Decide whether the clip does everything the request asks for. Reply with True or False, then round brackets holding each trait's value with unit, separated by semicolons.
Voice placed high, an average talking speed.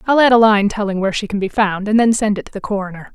False (210 Hz; 325 wpm)